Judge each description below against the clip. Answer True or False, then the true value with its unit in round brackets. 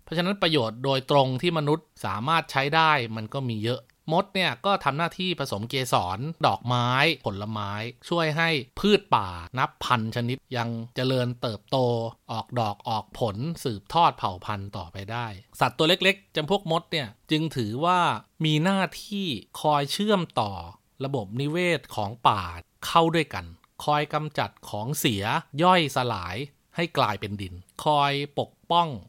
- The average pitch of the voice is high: False (135 Hz)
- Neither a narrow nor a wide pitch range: False (6.1 semitones)